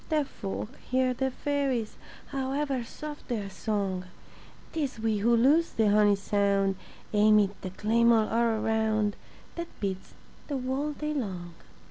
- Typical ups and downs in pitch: Yes, average, 4.6 semitones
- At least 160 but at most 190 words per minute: No, slow, 135 wpm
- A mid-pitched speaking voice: No, high, 225 Hz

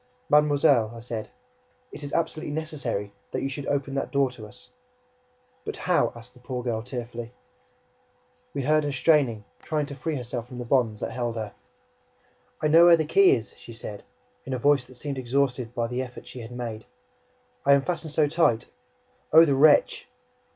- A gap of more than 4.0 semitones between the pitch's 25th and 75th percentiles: No, average, 3.7 semitones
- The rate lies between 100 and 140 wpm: No, average, 190 wpm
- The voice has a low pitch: Yes, low, 130 Hz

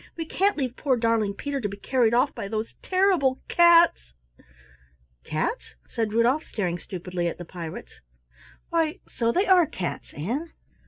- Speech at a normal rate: Yes, average, 155 wpm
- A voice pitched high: Yes, high, 240 Hz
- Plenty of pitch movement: Yes, wide, 8.3 semitones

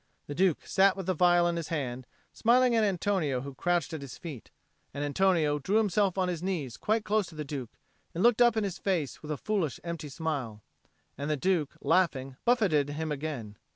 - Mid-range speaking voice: Yes, medium, 165 Hz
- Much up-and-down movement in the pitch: No, average, 5.0 semitones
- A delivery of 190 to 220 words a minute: Yes, fast, 205 wpm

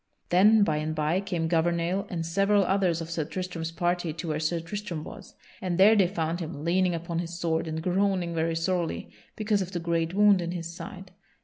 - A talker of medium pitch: Yes, medium, 175 Hz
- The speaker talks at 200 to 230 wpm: Yes, fast, 205 wpm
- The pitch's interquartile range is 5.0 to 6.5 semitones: No, narrow, 2.4 semitones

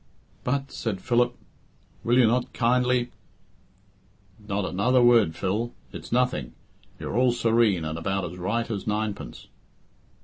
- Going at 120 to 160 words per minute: Yes, slow, 135 wpm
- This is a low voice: Yes, low, 110 Hz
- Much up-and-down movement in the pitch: No, average, 4.0 semitones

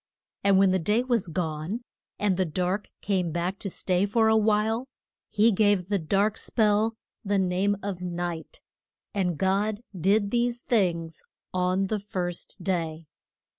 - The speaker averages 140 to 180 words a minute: Yes, average, 150 wpm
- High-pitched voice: Yes, high, 195 Hz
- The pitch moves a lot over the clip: No, average, 2.8 semitones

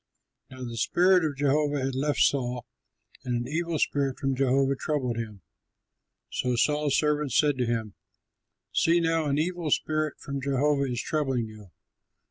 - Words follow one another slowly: No, average, 160 wpm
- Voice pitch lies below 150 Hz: Yes, medium, 140 Hz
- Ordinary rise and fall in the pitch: Yes, average, 3.2 semitones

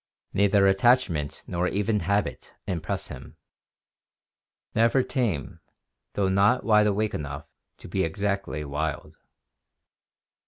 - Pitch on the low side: Yes, low, 100 Hz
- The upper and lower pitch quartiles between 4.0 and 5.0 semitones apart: Yes, average, 4.6 semitones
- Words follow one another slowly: Yes, slow, 105 wpm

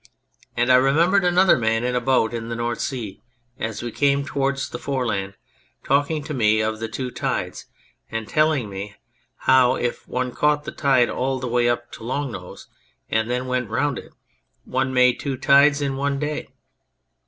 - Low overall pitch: Yes, low, 125 Hz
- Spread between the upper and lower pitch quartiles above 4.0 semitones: No, average, 3.1 semitones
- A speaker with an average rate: Yes, average, 185 wpm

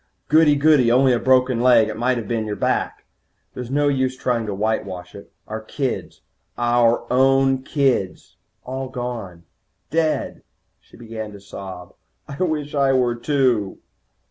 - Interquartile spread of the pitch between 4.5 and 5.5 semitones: No, average, 3.5 semitones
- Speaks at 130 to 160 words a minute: Yes, average, 150 wpm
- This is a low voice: Yes, low, 125 Hz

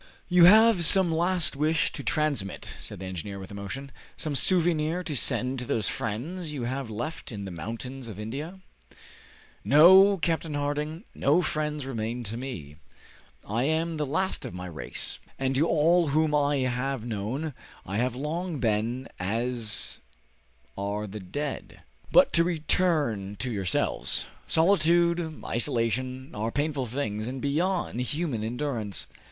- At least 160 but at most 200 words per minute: No, average, 145 wpm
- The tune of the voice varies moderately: No, wide, 6.1 semitones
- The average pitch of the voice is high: No, low, 135 Hz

